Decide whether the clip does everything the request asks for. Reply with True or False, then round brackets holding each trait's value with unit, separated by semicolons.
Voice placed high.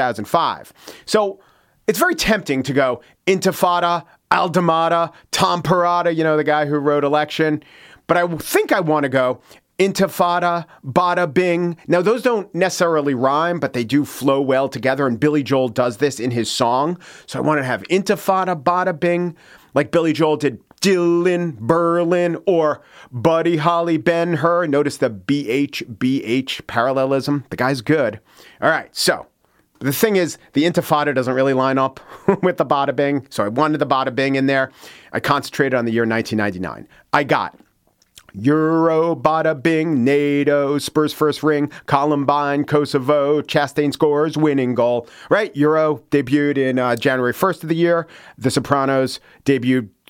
False (150 Hz)